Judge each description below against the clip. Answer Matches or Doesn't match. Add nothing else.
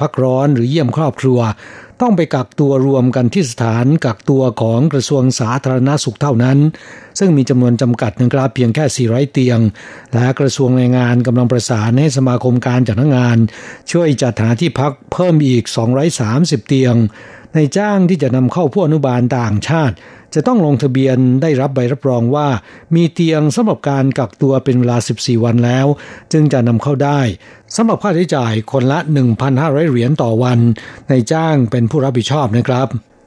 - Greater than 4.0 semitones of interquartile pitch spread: Doesn't match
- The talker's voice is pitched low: Matches